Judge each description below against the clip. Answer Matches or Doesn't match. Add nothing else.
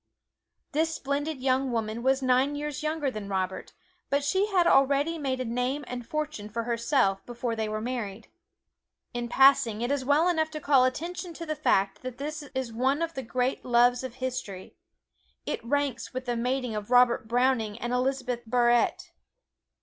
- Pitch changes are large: Doesn't match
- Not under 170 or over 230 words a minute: Matches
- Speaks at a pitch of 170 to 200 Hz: Doesn't match